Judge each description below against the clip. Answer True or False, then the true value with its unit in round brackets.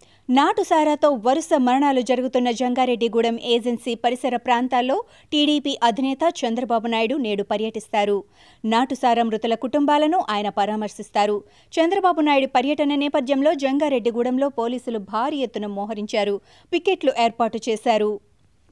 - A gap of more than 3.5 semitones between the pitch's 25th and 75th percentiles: True (4.1 semitones)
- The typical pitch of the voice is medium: False (245 Hz)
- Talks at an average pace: True (100 wpm)